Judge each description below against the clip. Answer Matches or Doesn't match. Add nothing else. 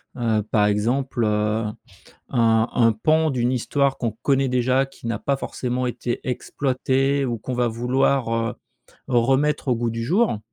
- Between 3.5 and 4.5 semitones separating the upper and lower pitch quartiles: Doesn't match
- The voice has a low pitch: Matches